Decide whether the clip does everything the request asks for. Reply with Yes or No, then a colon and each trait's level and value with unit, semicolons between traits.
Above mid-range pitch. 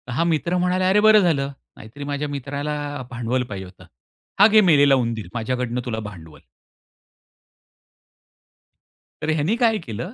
No: medium, 140 Hz